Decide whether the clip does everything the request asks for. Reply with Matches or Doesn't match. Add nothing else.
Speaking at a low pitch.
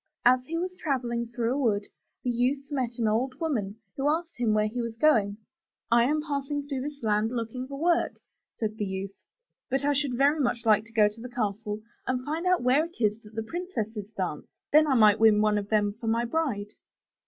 Doesn't match